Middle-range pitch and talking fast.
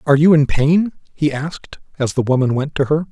Yes: medium, 145 Hz; fast, 230 wpm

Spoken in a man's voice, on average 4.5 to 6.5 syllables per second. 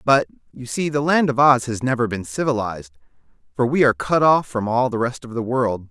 Yes: male; 5.7 syllables/s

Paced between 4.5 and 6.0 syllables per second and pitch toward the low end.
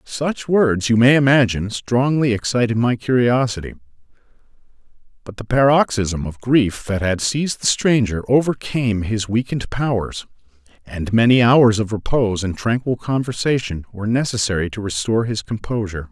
Yes: 5.2 syllables/s; low, 115 Hz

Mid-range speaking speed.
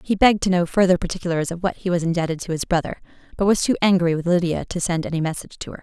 No: fast, 270 wpm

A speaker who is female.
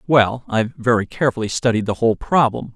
No: male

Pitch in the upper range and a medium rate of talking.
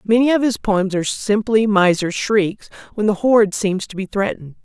Yes: high, 205 Hz; average, 195 wpm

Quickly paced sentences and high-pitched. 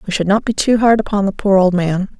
Yes: fast, 300 wpm; high, 200 Hz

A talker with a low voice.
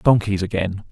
Yes: low, 100 Hz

